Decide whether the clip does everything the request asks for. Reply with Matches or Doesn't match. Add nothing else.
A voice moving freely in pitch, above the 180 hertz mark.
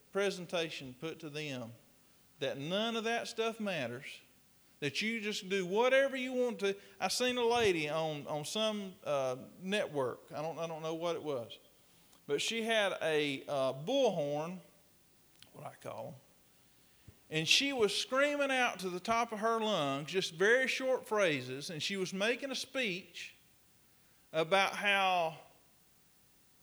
Matches